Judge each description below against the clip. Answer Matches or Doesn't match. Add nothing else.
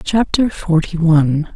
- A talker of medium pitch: Matches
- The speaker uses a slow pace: Matches